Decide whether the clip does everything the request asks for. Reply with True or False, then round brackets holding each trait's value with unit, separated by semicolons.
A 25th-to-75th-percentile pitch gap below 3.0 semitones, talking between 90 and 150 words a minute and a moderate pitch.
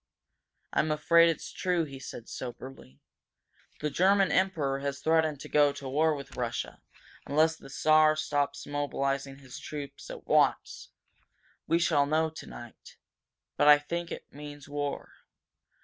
True (2.4 semitones; 140 wpm; 145 Hz)